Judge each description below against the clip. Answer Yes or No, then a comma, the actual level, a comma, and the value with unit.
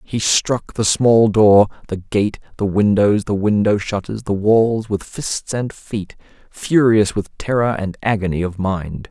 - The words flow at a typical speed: Yes, average, 165 wpm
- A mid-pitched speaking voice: No, low, 105 Hz